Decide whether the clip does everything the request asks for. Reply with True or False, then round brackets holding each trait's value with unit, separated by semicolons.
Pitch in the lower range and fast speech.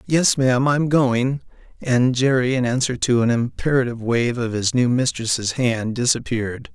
False (125 Hz; 160 wpm)